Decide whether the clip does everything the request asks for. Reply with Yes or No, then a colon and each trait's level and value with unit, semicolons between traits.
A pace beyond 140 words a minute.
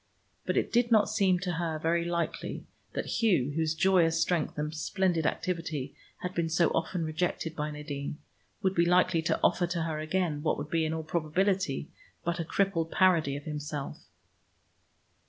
Yes: average, 175 wpm